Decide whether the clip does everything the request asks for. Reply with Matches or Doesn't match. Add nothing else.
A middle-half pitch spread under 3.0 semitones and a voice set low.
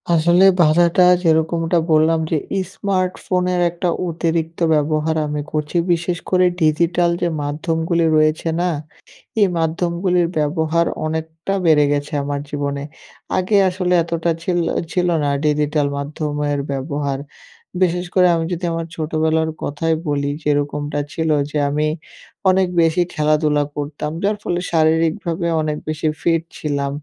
Doesn't match